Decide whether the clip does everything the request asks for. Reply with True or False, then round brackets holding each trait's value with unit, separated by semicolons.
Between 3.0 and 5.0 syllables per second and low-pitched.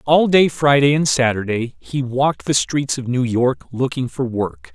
True (4.4 syllables/s; 130 Hz)